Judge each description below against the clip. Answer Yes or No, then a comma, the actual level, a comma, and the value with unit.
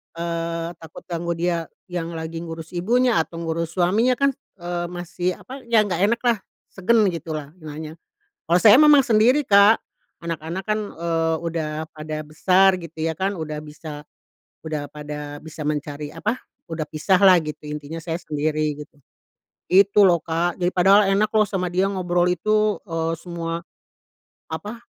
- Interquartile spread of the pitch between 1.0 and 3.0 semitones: No, average, 3.5 semitones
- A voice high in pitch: No, medium, 170 Hz